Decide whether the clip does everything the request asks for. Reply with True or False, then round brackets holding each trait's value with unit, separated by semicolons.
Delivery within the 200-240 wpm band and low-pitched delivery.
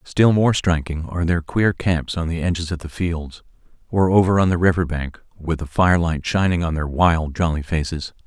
True (205 wpm; 85 Hz)